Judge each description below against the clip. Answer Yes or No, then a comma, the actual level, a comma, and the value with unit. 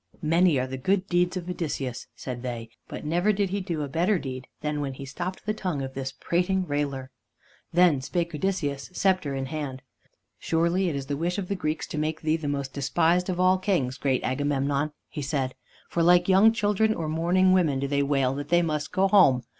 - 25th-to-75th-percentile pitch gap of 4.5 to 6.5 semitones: Yes, average, 4.8 semitones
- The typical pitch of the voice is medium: Yes, medium, 155 Hz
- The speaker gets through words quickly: Yes, fast, 210 wpm